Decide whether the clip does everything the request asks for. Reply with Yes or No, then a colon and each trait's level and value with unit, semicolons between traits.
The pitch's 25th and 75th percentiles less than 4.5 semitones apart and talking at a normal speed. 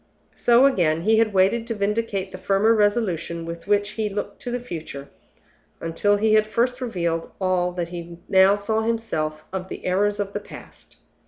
Yes: average, 3.9 semitones; average, 180 wpm